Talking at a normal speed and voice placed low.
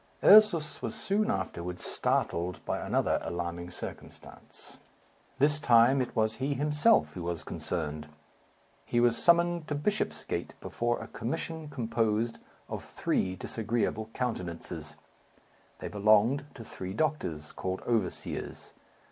No: slow, 120 wpm; low, 115 Hz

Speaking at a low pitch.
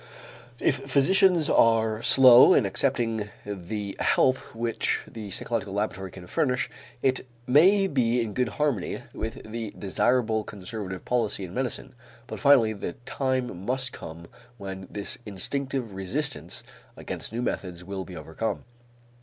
Yes: low, 115 Hz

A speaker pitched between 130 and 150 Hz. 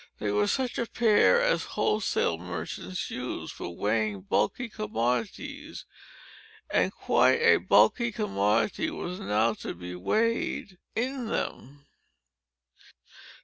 Yes: medium, 140 Hz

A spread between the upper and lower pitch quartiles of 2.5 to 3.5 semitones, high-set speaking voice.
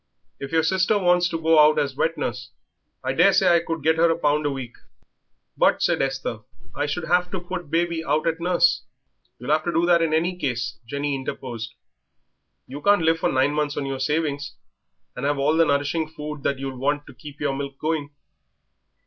No: average, 3.2 semitones; medium, 150 Hz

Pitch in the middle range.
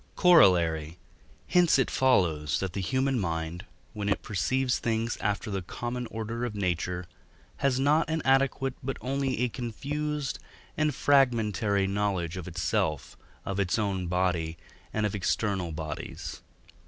No: low, 105 Hz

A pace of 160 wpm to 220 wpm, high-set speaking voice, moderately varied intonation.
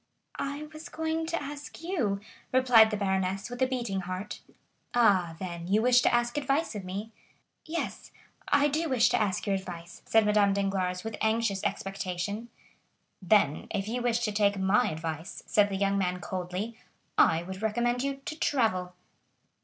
Yes: average, 170 wpm; high, 210 Hz; average, 4.6 semitones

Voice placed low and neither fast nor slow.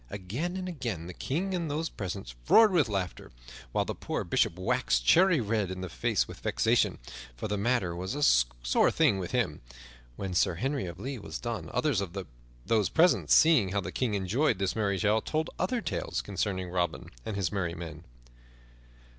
Yes: low, 100 Hz; average, 190 wpm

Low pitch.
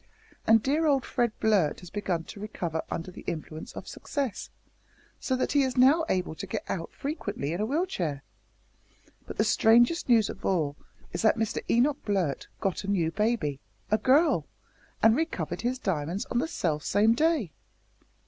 No: high, 215 Hz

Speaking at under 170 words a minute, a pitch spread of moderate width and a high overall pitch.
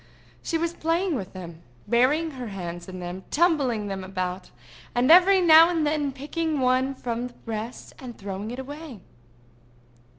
No: average, 155 wpm; wide, 8.3 semitones; very high, 255 Hz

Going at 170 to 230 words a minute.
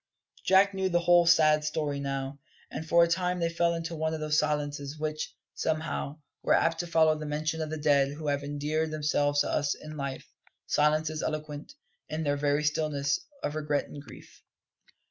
Yes: average, 185 wpm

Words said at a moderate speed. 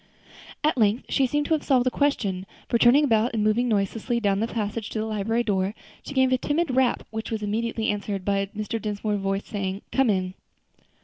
No: fast, 210 wpm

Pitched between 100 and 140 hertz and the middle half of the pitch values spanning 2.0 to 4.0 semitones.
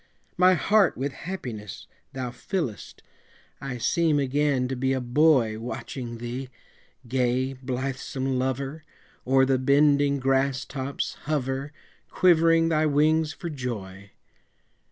Yes: low, 135 Hz; average, 2.9 semitones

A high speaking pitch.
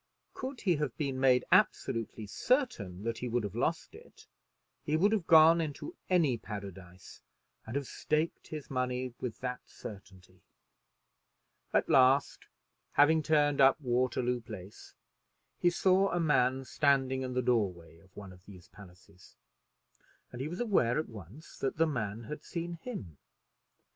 No: low, 130 Hz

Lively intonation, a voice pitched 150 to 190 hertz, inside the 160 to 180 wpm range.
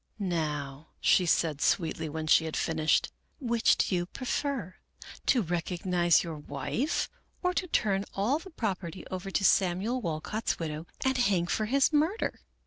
Yes: wide, 6.5 semitones; medium, 185 Hz; average, 165 wpm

